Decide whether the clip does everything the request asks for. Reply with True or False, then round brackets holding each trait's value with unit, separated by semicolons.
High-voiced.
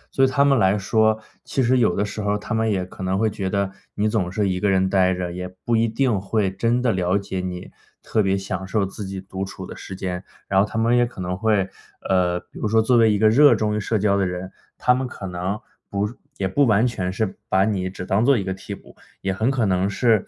False (100 Hz)